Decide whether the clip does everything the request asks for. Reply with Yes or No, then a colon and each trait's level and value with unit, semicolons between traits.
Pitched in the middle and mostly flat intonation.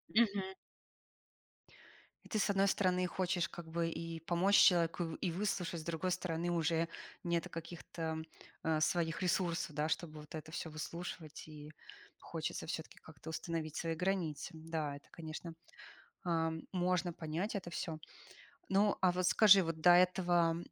Yes: medium, 170 Hz; narrow, 2.1 semitones